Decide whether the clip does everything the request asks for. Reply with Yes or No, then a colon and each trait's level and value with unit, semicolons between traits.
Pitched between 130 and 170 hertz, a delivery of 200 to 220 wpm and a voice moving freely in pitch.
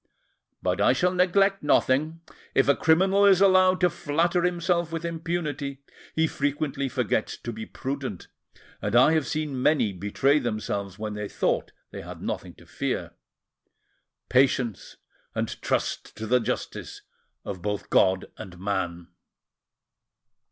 No: medium, 140 Hz; slow, 135 wpm; wide, 7.9 semitones